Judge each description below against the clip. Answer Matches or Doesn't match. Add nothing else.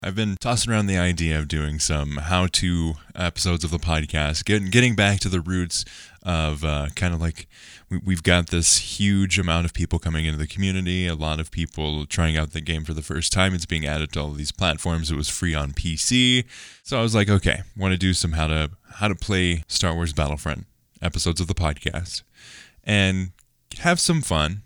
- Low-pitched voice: Matches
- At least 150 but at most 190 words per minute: Doesn't match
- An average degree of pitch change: Matches